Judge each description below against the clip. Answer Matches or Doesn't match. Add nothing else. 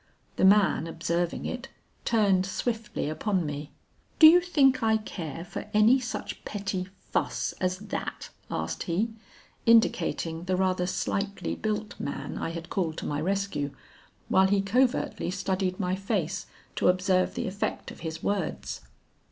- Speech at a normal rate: Matches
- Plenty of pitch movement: Doesn't match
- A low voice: Doesn't match